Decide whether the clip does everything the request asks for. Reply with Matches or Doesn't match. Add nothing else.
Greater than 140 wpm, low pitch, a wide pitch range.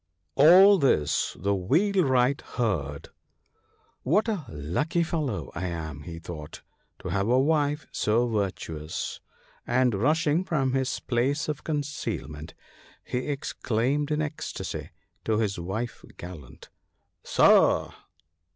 Doesn't match